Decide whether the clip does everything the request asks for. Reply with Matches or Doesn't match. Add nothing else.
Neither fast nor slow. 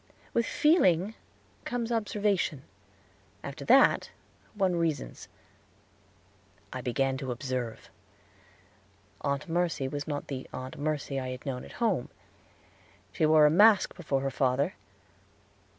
Doesn't match